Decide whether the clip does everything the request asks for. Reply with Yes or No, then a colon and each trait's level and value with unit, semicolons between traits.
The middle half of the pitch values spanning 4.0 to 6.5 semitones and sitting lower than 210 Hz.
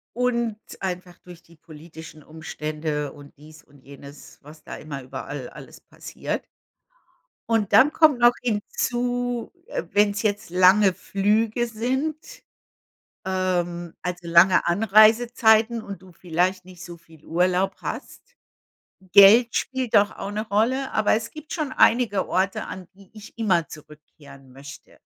Yes: wide, 5.4 semitones; high, 190 Hz